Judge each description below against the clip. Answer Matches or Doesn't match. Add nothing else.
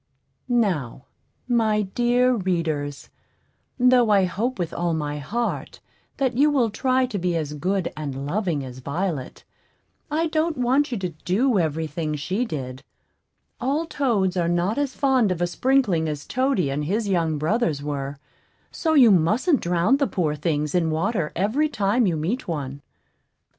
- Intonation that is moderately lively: Doesn't match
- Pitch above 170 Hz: Matches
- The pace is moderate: Matches